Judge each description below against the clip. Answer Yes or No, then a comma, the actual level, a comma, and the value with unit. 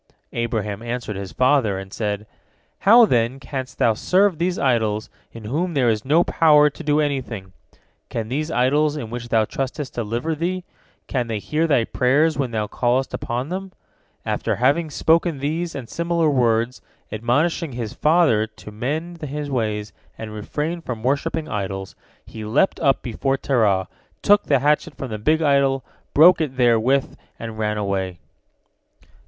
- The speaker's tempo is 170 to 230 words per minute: No, average, 160 wpm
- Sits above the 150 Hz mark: No, low, 130 Hz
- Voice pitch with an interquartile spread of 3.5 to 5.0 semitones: No, wide, 5.5 semitones